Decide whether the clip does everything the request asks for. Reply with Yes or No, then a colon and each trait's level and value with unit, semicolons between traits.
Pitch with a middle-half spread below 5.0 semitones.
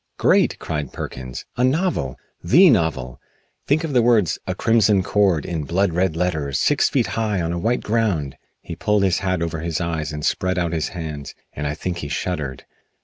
No: average, 5.3 semitones